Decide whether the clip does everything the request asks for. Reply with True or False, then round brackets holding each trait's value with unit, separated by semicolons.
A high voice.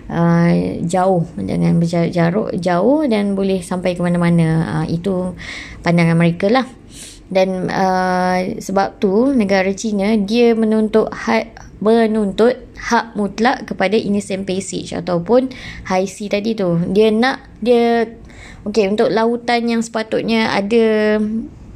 True (200 Hz)